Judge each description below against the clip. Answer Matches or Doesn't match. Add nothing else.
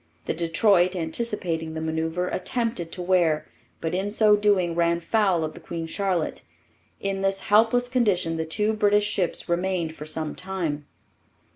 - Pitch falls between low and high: Matches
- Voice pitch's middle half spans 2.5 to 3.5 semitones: Doesn't match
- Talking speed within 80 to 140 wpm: Doesn't match